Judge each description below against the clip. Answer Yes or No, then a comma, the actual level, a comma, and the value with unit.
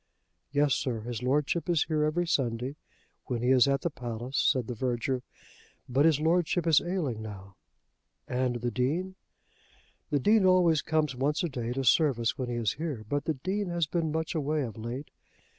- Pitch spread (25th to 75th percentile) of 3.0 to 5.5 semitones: Yes, average, 4.7 semitones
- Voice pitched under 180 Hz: Yes, medium, 140 Hz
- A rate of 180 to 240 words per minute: Yes, average, 185 wpm